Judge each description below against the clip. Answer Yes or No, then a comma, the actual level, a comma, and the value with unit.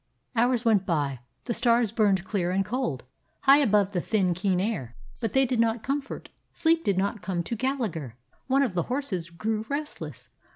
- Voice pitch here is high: Yes, high, 215 Hz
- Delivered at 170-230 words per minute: Yes, average, 180 wpm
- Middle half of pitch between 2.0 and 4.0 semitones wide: No, wide, 5.4 semitones